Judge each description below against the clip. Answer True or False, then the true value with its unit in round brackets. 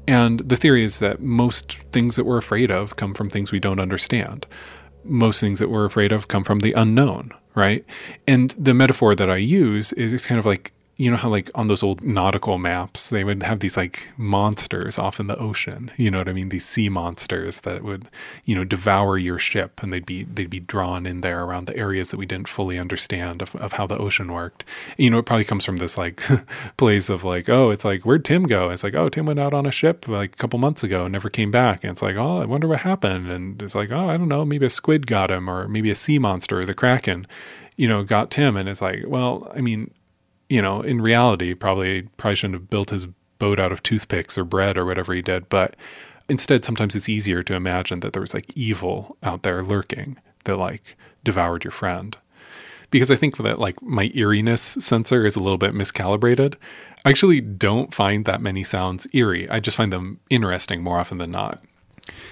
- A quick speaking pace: True (230 wpm)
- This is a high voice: False (105 Hz)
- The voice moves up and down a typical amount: True (4.4 semitones)